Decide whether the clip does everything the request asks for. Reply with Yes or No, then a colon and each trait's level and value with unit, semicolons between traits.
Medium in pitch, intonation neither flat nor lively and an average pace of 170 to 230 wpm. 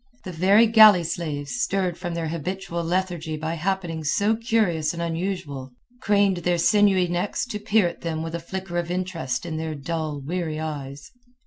Yes: medium, 170 Hz; average, 3.2 semitones; average, 175 wpm